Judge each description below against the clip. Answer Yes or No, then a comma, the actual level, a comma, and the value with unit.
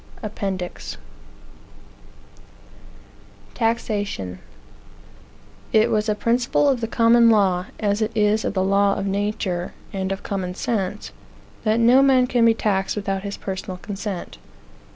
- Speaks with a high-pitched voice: Yes, high, 205 Hz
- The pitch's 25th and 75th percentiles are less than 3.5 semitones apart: Yes, average, 2.9 semitones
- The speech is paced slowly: Yes, slow, 130 wpm